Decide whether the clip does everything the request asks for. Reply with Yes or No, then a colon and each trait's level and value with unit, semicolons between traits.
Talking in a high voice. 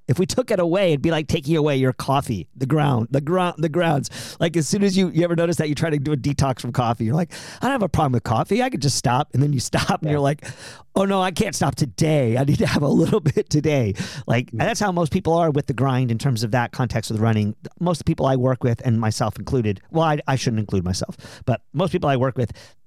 No: medium, 140 Hz